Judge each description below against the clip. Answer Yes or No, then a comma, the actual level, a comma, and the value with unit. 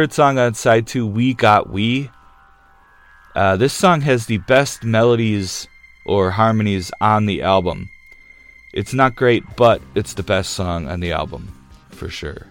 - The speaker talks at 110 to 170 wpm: Yes, average, 155 wpm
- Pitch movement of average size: No, wide, 6.3 semitones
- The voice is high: No, low, 105 Hz